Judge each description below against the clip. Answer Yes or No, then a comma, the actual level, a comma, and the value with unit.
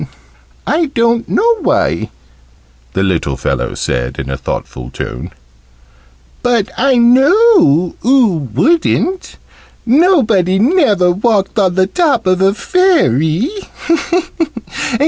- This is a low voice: No, high, 220 Hz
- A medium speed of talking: No, slow, 105 wpm